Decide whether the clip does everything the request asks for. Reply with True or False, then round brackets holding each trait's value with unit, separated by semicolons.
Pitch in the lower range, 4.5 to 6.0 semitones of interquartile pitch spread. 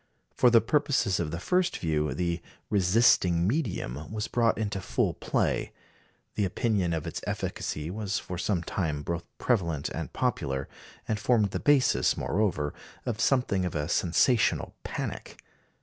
True (95 Hz; 5.4 semitones)